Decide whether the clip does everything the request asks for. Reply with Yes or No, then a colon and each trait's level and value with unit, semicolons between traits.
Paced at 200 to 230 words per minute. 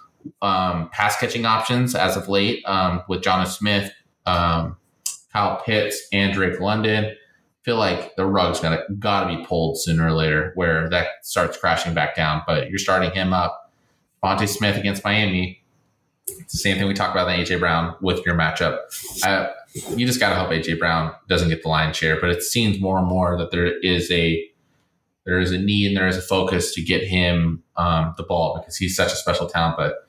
Yes: fast, 205 wpm